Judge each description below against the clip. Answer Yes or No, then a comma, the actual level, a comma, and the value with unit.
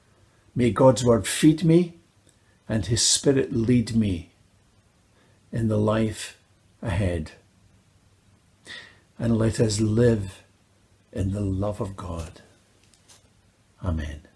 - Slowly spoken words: Yes, slow, 100 wpm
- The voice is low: Yes, low, 105 Hz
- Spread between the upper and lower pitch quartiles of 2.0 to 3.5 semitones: Yes, narrow, 2.6 semitones